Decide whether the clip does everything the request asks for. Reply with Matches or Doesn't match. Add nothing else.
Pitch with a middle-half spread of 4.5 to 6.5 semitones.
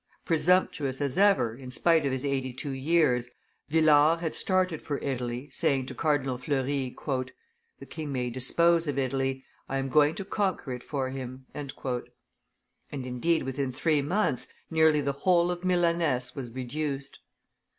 Doesn't match